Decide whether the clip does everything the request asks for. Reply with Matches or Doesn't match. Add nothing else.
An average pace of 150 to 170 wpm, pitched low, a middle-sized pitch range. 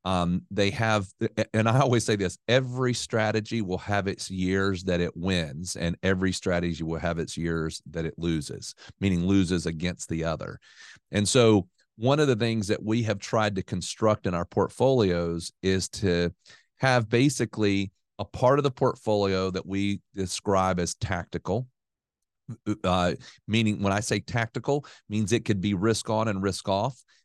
Matches